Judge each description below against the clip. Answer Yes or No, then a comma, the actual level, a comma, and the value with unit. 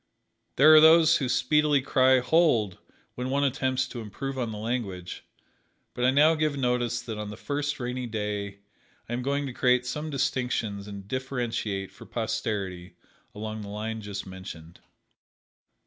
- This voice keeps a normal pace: Yes, average, 160 wpm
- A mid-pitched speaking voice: No, low, 125 Hz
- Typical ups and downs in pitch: Yes, average, 4.5 semitones